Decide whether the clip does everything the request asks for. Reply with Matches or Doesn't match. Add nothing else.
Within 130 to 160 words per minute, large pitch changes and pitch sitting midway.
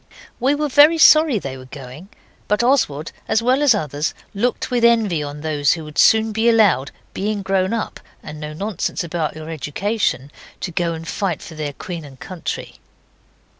Doesn't match